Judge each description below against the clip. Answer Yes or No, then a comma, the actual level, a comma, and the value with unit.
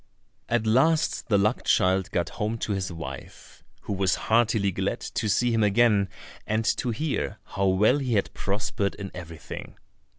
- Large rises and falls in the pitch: No, average, 3.1 semitones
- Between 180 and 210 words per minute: No, average, 165 wpm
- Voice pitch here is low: Yes, low, 105 Hz